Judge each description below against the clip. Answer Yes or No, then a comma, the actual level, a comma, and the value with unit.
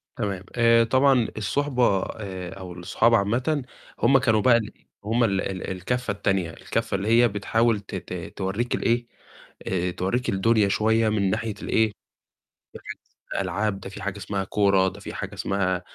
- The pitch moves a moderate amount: Yes, average, 3.4 semitones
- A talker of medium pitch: No, low, 105 Hz